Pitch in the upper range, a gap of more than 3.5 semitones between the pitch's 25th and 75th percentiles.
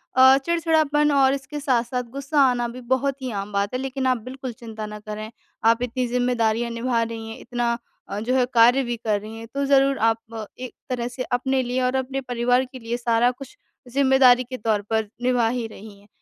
No: high, 245 Hz; narrow, 2.5 semitones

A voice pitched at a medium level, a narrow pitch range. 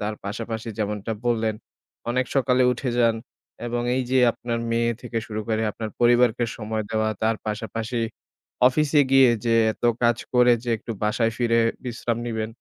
No: low, 115 Hz; narrow, 1.7 semitones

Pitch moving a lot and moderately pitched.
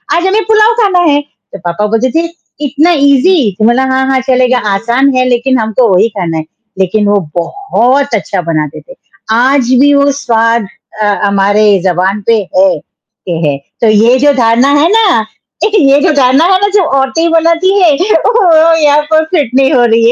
No: wide, 6.3 semitones; very high, 260 Hz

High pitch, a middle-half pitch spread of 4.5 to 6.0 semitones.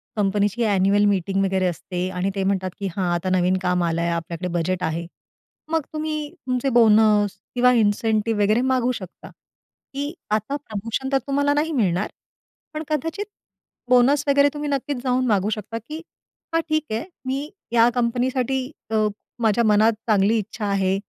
Yes: high, 220 Hz; average, 5.2 semitones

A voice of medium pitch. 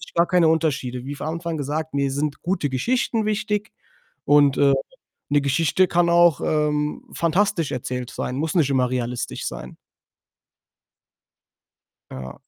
Yes: medium, 150 Hz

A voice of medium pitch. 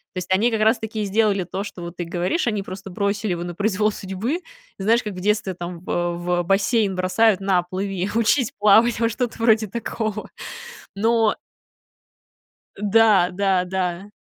No: high, 200 Hz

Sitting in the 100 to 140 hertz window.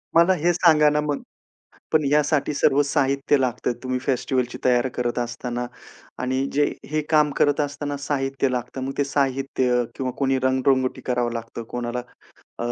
Yes: low, 135 Hz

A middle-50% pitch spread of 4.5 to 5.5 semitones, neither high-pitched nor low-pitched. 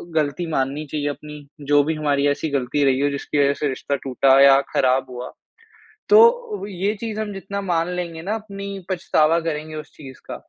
Yes: average, 5.2 semitones; medium, 150 Hz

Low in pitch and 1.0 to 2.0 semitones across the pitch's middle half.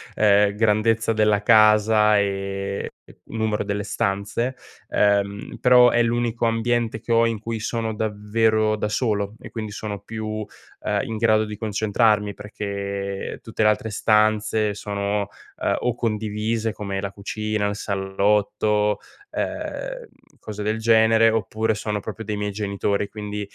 Yes: low, 105 Hz; narrow, 1.5 semitones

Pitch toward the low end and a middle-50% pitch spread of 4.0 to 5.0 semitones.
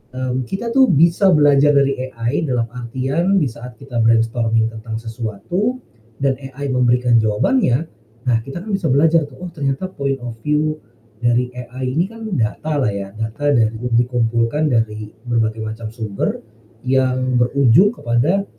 Yes: low, 125 Hz; average, 4.3 semitones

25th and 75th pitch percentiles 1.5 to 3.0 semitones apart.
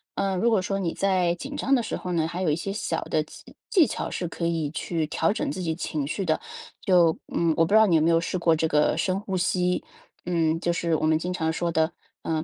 Yes: average, 2.7 semitones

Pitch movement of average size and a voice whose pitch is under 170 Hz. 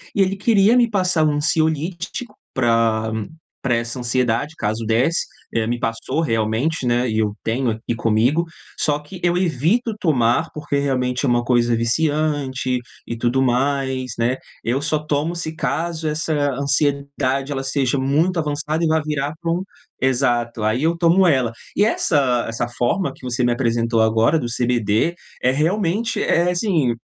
Yes: average, 5.0 semitones; low, 135 Hz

